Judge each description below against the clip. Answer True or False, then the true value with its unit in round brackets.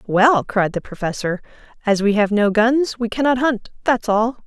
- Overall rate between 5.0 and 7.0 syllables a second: False (4.6 syllables/s)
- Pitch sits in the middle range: False (225 Hz)